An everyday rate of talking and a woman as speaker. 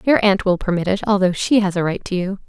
No: fast, 290 wpm; female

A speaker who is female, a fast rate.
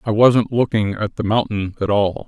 No: male; fast, 210 wpm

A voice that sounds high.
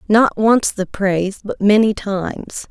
Yes: high, 205 Hz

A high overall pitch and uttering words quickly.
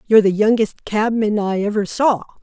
No: high, 210 Hz; average, 175 wpm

